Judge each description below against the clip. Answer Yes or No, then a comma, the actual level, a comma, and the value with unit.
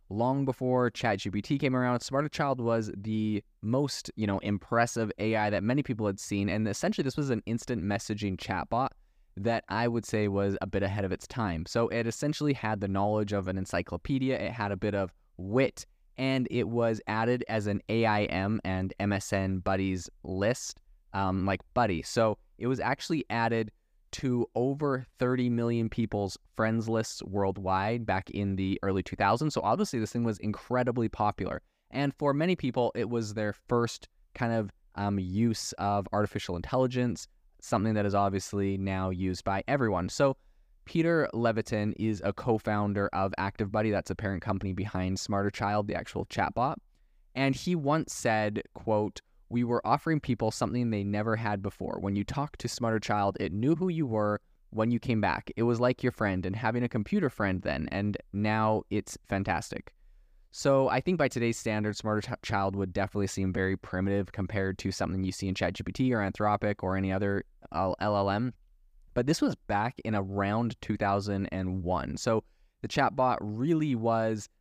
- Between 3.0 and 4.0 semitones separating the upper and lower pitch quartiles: Yes, average, 3.4 semitones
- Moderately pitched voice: No, low, 105 Hz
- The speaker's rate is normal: Yes, average, 175 wpm